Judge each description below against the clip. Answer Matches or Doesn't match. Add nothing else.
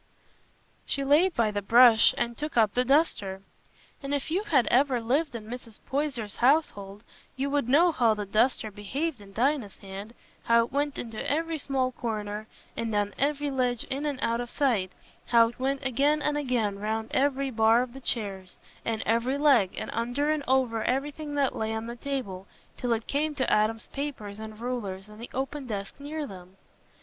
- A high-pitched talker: Matches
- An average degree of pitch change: Matches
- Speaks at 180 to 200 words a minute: Matches